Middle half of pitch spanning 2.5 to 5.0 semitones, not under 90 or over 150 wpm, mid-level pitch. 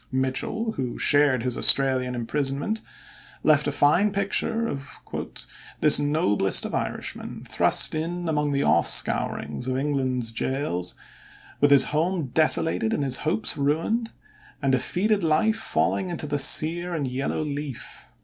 Yes: average, 4.1 semitones; average, 140 wpm; medium, 145 Hz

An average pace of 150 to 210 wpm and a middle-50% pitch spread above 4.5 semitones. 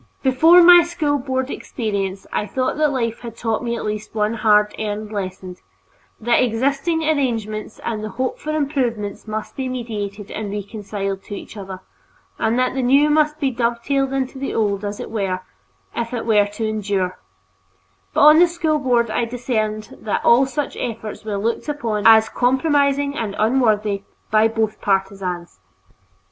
No: average, 165 wpm; average, 4.2 semitones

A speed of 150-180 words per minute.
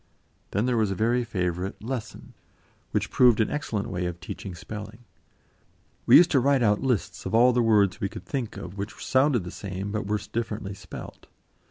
No: average, 190 wpm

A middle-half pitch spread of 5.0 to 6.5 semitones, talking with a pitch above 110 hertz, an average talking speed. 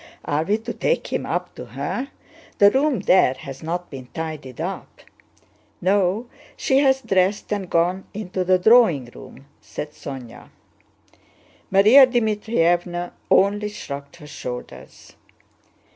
No: wide, 5.5 semitones; medium, 185 Hz; slow, 130 wpm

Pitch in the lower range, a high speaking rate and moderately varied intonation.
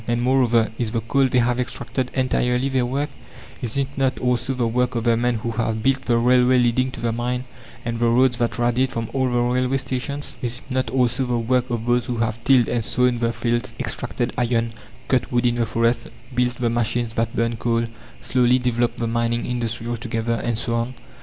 No: low, 120 Hz; fast, 215 wpm; narrow, 1.4 semitones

